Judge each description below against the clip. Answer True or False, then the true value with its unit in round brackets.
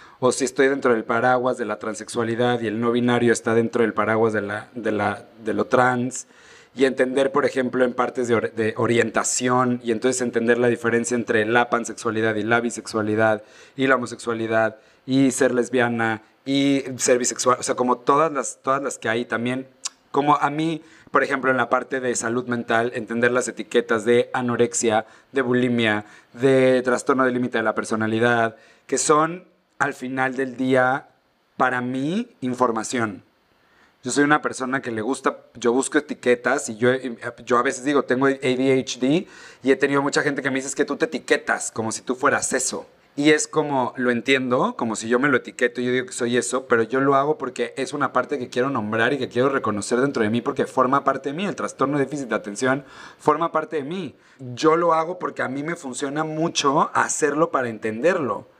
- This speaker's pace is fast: True (200 wpm)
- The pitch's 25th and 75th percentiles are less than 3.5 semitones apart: True (2.5 semitones)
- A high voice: False (125 Hz)